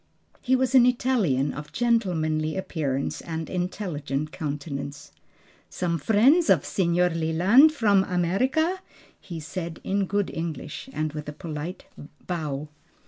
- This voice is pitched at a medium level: Yes, medium, 170 Hz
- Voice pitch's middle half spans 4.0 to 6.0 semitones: Yes, average, 5.2 semitones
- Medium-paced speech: No, slow, 125 wpm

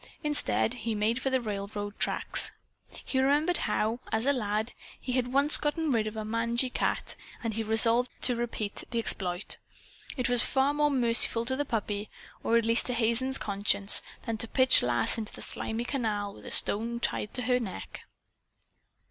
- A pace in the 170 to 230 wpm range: Yes, average, 180 wpm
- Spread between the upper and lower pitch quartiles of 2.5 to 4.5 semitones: Yes, average, 3.3 semitones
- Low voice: No, high, 230 Hz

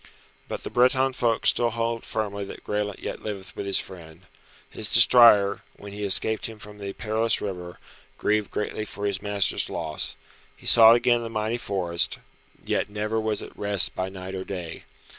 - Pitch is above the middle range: No, low, 105 Hz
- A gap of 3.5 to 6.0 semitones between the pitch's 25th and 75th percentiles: No, narrow, 2.6 semitones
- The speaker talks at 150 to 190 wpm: Yes, average, 180 wpm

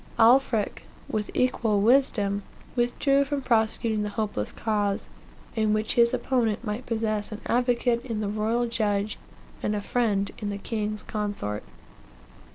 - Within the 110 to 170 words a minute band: Yes, average, 140 wpm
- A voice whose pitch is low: No, high, 220 Hz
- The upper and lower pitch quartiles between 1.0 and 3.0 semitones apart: Yes, narrow, 2.4 semitones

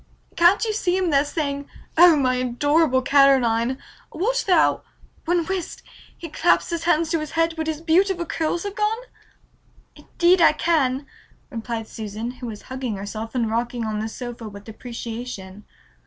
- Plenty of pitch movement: Yes, wide, 6.2 semitones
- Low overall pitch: No, very high, 280 Hz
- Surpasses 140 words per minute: Yes, average, 165 wpm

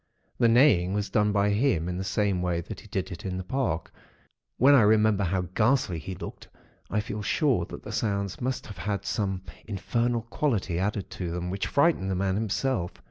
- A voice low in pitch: Yes, low, 100 Hz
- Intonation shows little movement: No, average, 3.6 semitones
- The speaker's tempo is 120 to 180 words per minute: No, average, 200 wpm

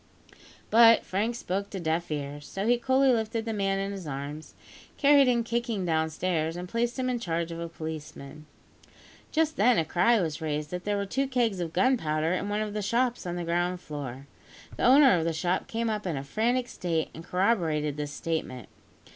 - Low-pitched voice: No, medium, 185 Hz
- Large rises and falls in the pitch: Yes, wide, 6.5 semitones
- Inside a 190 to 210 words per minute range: Yes, average, 200 wpm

